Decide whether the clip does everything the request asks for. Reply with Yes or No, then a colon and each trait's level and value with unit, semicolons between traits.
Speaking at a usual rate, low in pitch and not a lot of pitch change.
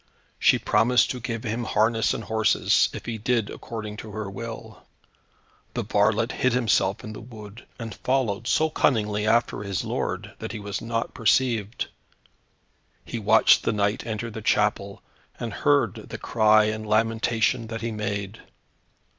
Yes: average, 155 wpm; low, 110 Hz; narrow, 1.8 semitones